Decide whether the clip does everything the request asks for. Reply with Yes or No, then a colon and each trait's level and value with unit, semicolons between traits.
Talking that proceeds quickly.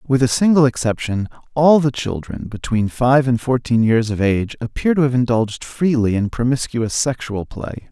No: average, 175 wpm